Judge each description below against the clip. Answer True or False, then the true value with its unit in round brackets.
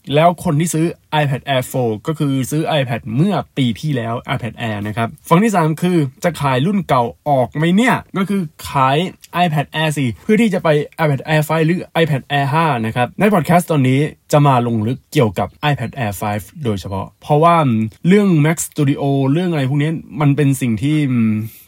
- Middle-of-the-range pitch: True (145 Hz)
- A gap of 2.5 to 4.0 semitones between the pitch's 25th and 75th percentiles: False (4.9 semitones)